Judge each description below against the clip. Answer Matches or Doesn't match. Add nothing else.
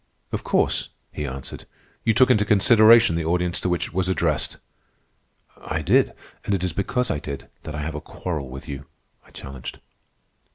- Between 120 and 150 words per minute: Doesn't match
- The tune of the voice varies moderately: Doesn't match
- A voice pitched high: Doesn't match